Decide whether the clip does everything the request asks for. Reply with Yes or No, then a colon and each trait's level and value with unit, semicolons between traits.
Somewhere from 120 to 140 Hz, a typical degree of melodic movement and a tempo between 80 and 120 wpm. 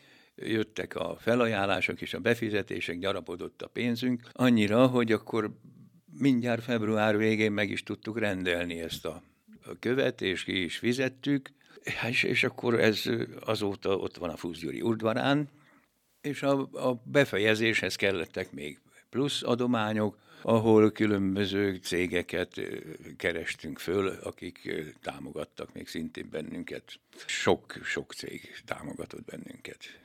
No: low, 110 Hz; average, 3.1 semitones; average, 115 wpm